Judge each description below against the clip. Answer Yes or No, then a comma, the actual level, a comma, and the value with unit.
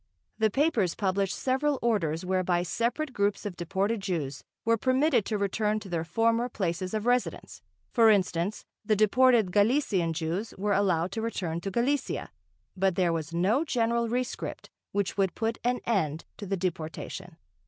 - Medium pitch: No, high, 200 Hz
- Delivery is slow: No, average, 160 wpm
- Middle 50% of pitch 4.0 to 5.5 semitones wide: Yes, average, 4.3 semitones